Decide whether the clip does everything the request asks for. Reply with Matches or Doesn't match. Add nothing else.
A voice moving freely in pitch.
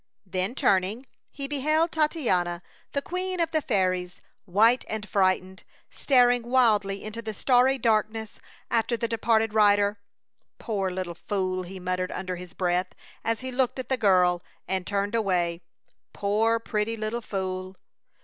Doesn't match